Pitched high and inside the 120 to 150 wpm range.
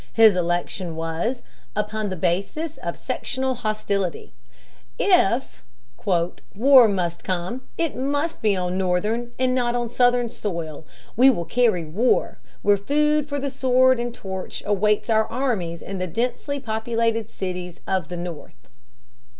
Yes: high, 215 Hz; average, 140 wpm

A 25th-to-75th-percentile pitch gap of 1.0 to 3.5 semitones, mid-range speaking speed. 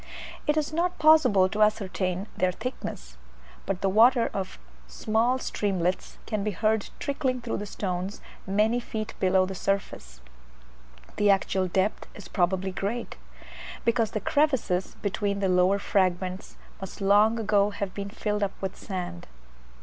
Yes: average, 2.8 semitones; average, 145 wpm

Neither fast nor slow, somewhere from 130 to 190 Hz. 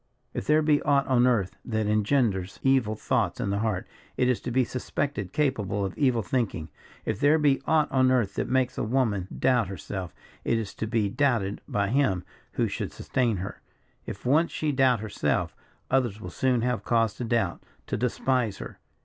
No: average, 190 wpm; low, 115 Hz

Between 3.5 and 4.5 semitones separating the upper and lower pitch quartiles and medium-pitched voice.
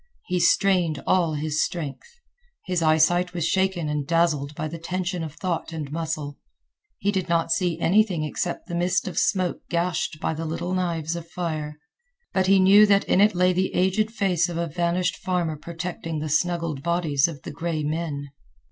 No: narrow, 2.6 semitones; medium, 170 Hz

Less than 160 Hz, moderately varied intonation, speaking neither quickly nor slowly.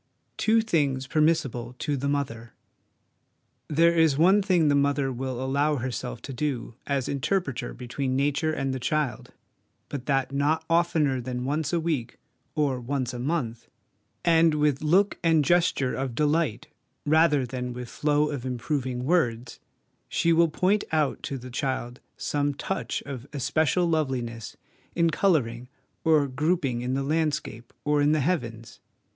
Yes: medium, 140 Hz; average, 3.7 semitones; average, 150 wpm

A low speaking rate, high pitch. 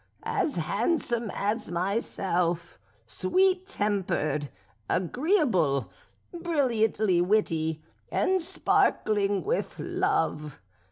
Yes: slow, 70 wpm; high, 205 Hz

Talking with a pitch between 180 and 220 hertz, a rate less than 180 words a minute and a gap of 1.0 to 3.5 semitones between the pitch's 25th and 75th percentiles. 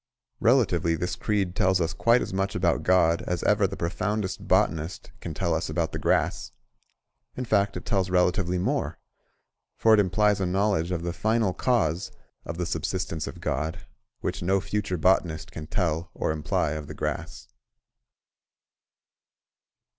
No: very low, 90 Hz; average, 155 wpm; average, 2.8 semitones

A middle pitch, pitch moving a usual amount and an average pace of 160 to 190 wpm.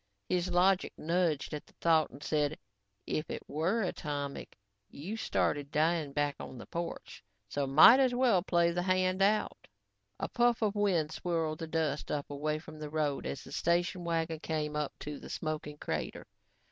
Yes: medium, 160 Hz; average, 3.3 semitones; average, 175 wpm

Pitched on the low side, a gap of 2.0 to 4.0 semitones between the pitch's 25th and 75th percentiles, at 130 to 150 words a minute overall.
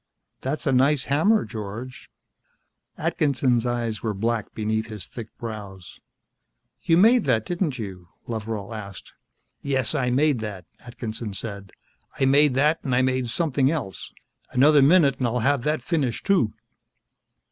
No: low, 125 Hz; average, 4.5 semitones; average, 145 wpm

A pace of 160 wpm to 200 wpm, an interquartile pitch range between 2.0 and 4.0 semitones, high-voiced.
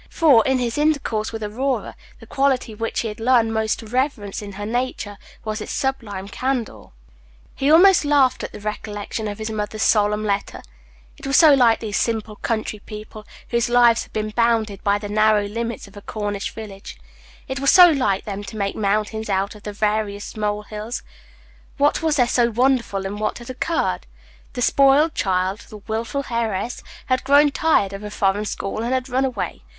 Yes: average, 190 wpm; average, 3.6 semitones; high, 220 Hz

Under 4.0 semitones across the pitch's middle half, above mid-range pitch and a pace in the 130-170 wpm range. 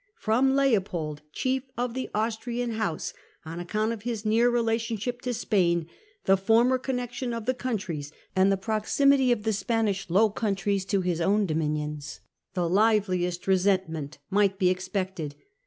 No: average, 4.3 semitones; high, 205 Hz; average, 160 wpm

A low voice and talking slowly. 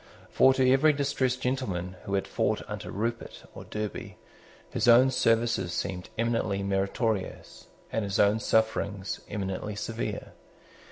Yes: low, 110 Hz; slow, 130 wpm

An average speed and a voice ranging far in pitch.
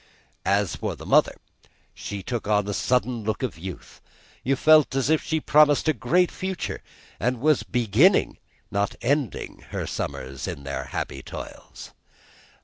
Yes: average, 150 wpm; wide, 6.8 semitones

